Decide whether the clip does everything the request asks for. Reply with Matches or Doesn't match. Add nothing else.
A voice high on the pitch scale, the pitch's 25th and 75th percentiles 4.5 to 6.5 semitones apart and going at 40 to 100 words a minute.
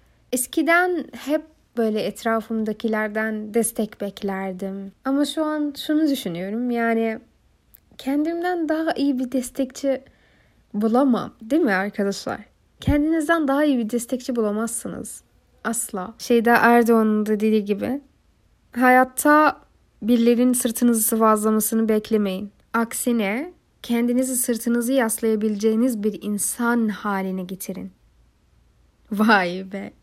Doesn't match